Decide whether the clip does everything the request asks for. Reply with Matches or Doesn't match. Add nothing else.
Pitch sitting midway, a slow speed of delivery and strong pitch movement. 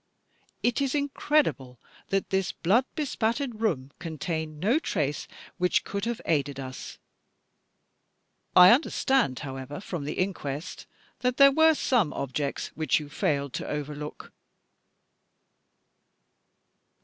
Matches